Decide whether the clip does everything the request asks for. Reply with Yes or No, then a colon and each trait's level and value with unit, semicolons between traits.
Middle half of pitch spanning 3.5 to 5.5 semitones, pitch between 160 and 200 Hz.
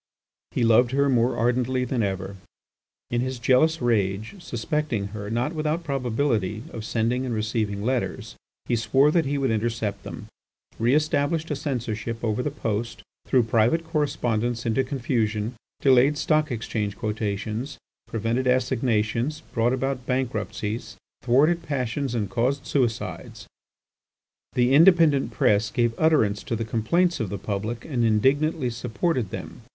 No: average, 3.9 semitones; low, 120 Hz